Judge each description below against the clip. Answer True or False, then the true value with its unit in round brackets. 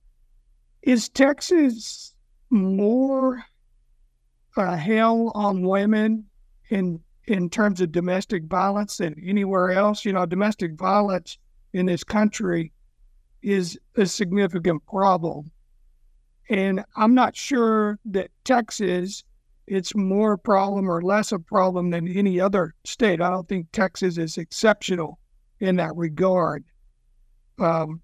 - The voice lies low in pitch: False (190 Hz)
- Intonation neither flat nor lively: True (3.3 semitones)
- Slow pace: True (120 wpm)